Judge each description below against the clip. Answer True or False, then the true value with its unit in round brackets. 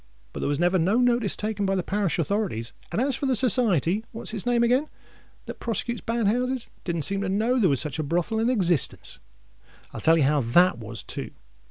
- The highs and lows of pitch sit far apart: True (6.0 semitones)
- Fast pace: True (215 wpm)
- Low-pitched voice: False (200 Hz)